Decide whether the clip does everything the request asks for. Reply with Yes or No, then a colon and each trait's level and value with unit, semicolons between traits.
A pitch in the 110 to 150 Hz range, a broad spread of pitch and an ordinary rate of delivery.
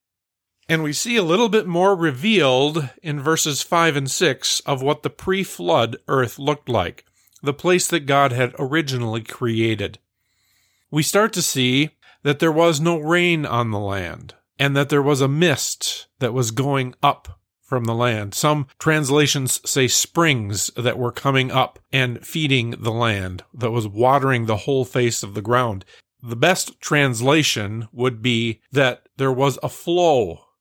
No: low, 135 Hz; average, 4.5 semitones; average, 165 wpm